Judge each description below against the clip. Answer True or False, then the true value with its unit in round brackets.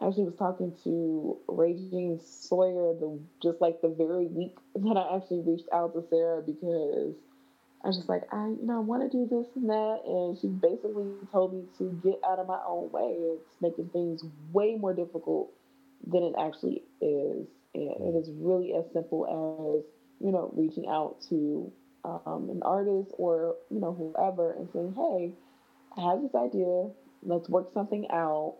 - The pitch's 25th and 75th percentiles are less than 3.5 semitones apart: True (3.1 semitones)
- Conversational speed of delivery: True (180 wpm)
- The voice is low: False (180 Hz)